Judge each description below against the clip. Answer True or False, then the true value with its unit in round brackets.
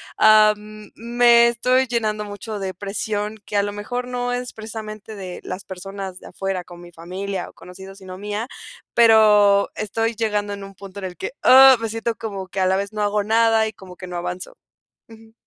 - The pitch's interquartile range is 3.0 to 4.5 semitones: False (2.6 semitones)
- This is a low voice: False (210 Hz)